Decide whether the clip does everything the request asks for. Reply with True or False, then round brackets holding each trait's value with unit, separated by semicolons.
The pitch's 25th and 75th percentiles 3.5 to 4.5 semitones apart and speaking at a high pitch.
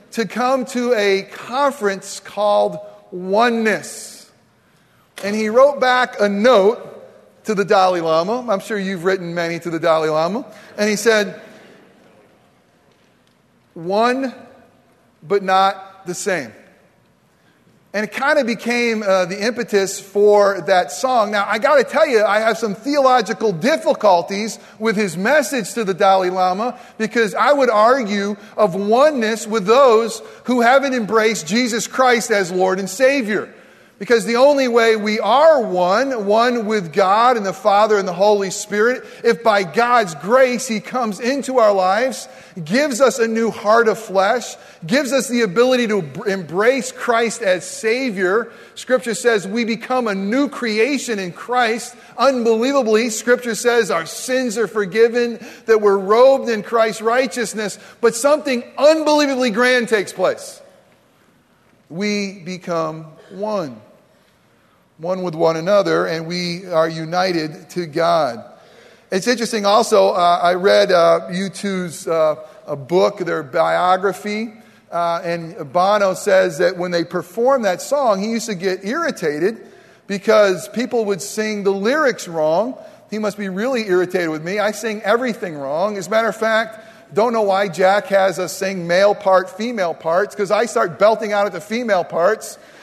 True (3.8 semitones; 215 Hz)